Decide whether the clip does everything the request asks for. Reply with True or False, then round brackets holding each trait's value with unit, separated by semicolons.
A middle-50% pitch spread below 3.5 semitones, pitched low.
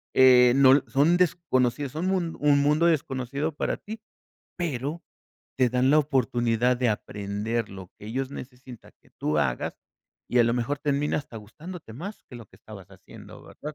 False (4.2 semitones; 130 Hz)